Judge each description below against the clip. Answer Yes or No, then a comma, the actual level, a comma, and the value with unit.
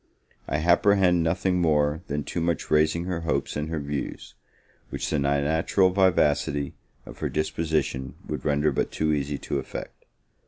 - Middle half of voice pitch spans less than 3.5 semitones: Yes, average, 2.8 semitones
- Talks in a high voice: No, very low, 80 Hz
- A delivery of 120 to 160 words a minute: Yes, average, 155 wpm